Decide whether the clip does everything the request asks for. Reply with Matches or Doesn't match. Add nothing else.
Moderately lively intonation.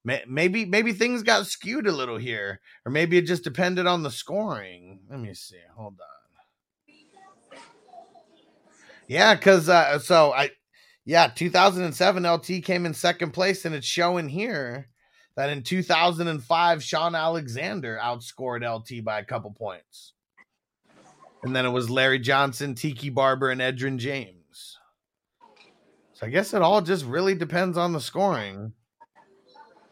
Doesn't match